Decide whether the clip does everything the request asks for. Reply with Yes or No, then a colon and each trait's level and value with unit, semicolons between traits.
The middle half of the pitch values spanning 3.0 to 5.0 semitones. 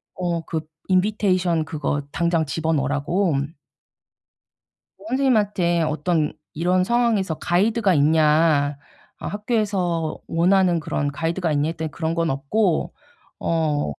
Yes: average, 3.4 semitones